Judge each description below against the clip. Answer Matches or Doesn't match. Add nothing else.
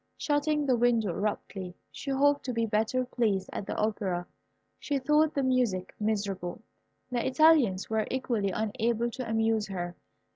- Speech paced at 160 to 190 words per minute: Doesn't match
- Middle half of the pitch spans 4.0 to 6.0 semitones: Matches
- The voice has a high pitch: Matches